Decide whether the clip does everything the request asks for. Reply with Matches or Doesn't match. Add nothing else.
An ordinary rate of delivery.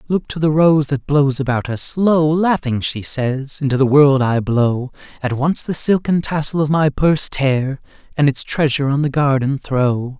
Matches